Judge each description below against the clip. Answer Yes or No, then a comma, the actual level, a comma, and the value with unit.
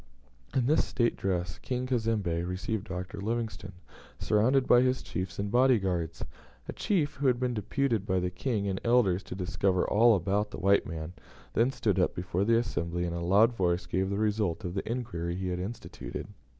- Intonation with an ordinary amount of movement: Yes, average, 4.6 semitones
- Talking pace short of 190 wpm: No, average, 195 wpm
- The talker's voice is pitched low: Yes, low, 100 Hz